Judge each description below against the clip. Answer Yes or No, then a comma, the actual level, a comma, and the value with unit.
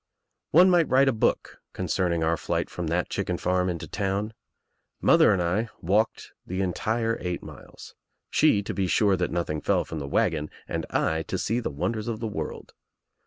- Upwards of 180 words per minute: Yes, average, 190 wpm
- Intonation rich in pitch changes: No, average, 4.5 semitones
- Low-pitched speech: Yes, very low, 95 Hz